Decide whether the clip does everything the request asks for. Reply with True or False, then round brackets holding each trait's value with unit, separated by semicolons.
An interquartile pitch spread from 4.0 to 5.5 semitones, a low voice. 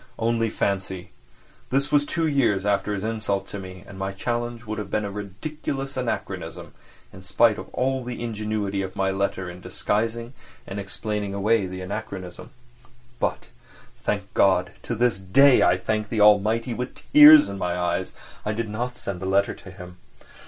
False (3.4 semitones; 105 Hz)